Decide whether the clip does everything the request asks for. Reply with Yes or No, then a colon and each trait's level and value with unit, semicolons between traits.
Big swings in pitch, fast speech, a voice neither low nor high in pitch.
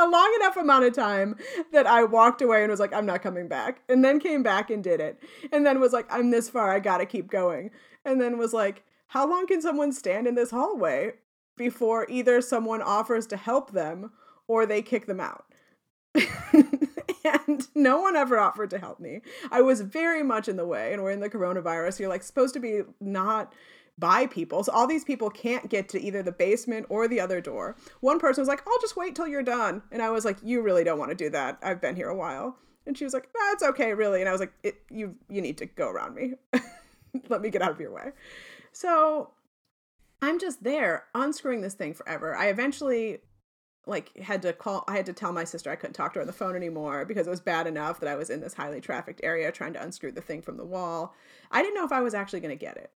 No: wide, 5.8 semitones; fast, 245 wpm; high, 235 Hz